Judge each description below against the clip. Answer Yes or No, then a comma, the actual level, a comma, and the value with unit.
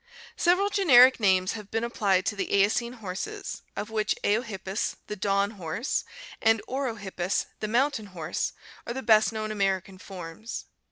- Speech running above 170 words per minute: No, average, 155 wpm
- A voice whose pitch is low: No, high, 215 Hz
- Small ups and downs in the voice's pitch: No, average, 3.6 semitones